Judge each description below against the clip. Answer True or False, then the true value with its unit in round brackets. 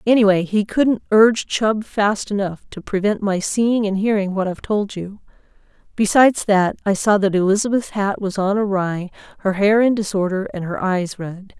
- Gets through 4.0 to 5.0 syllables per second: True (4.9 syllables/s)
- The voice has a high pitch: True (200 Hz)